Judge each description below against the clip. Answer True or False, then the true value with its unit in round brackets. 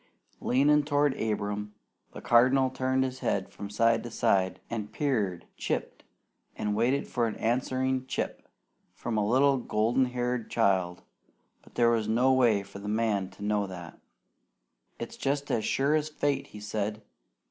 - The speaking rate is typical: True (160 wpm)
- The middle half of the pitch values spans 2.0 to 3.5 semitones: False (4.0 semitones)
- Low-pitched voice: True (115 Hz)